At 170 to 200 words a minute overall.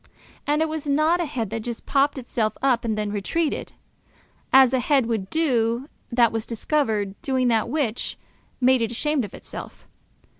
Yes: average, 175 wpm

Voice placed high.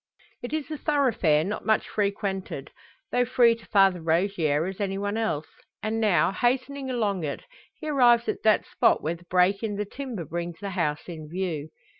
Yes: high, 200 Hz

